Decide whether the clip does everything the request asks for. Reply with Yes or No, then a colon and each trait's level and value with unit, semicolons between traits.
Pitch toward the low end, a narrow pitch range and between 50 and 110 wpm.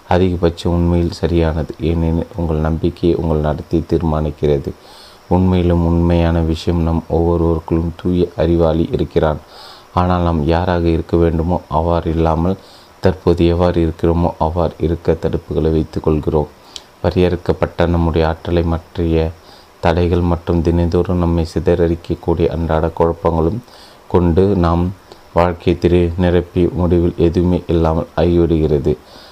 Yes: very low, 85 Hz; narrow, 1.2 semitones; average, 100 wpm